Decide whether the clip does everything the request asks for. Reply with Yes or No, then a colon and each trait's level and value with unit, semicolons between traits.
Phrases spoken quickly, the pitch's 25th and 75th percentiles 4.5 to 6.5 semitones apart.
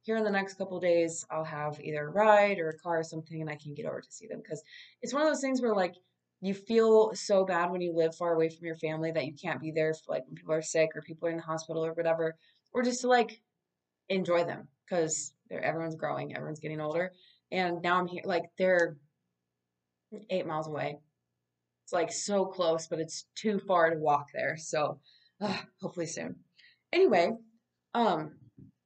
No: fast, 210 wpm; average, 3.6 semitones